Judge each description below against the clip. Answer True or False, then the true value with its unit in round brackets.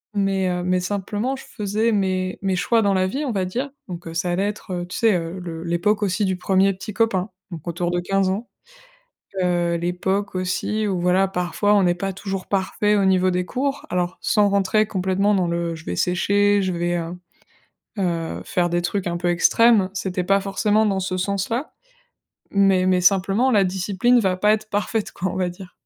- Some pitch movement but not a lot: False (2.3 semitones)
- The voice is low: False (190 Hz)